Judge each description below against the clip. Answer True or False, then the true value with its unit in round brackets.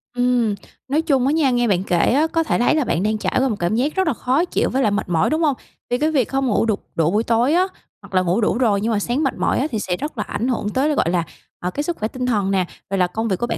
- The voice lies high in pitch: True (240 Hz)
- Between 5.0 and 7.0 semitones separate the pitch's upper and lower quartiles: True (5.4 semitones)